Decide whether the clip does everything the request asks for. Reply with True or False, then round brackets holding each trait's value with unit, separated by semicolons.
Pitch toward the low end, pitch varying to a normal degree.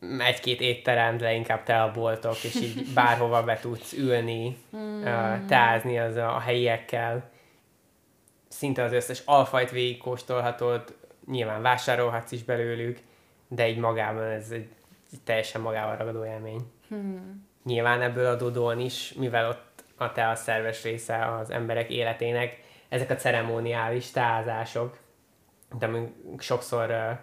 False (120 Hz; 1.3 semitones)